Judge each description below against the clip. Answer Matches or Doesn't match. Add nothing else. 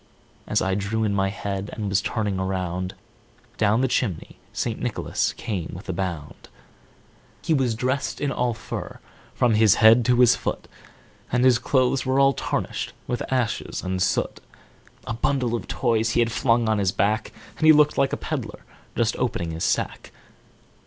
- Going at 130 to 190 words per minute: Matches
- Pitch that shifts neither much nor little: Matches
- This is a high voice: Doesn't match